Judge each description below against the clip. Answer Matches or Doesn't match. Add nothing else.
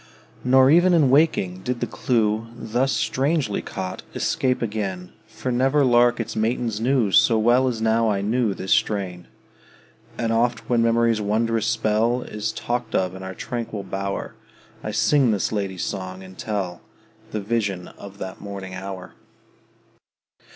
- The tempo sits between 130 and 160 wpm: Matches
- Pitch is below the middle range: Matches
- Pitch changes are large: Doesn't match